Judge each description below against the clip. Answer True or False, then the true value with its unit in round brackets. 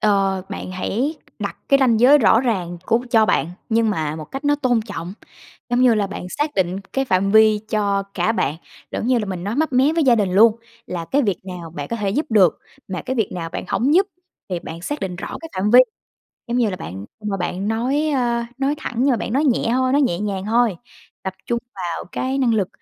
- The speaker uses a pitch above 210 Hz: True (220 Hz)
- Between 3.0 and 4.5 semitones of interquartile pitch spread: False (5.3 semitones)